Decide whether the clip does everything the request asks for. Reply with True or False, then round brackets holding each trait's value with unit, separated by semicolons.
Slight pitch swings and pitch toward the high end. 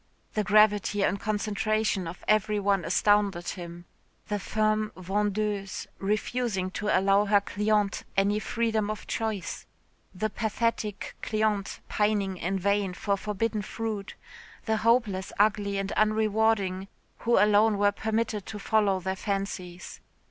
True (1.6 semitones; 205 Hz)